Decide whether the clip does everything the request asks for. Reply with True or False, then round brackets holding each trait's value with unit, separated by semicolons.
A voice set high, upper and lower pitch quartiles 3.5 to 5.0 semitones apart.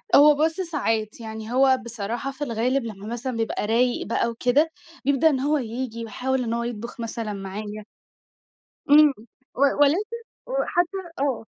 True (245 Hz; 4.0 semitones)